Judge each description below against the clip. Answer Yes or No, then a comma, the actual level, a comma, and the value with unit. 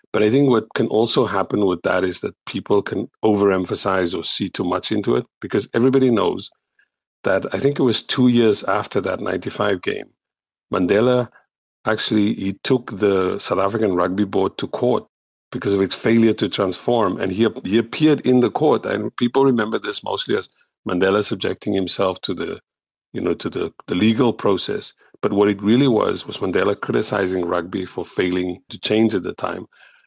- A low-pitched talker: Yes, low, 110 Hz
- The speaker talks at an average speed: Yes, average, 185 wpm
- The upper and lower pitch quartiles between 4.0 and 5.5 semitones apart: Yes, average, 4.3 semitones